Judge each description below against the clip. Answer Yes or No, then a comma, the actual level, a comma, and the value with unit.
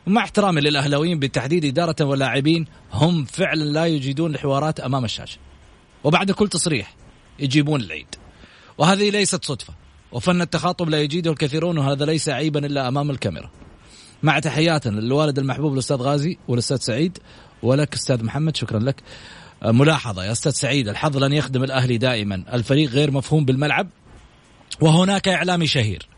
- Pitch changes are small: No, average, 4.1 semitones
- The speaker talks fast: Yes, fast, 140 wpm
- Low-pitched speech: No, medium, 145 Hz